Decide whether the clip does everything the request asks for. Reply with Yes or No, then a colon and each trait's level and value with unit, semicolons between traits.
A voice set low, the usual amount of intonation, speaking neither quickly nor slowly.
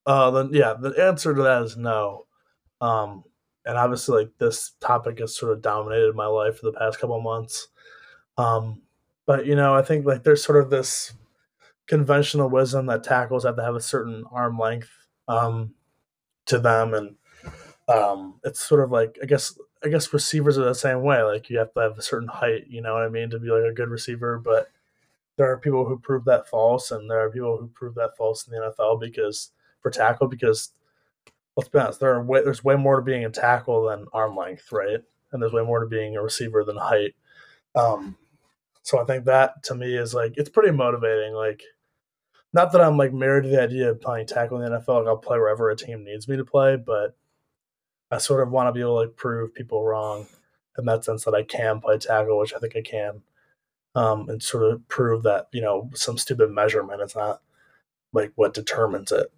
No: low, 120 Hz; average, 3.5 semitones; fast, 220 wpm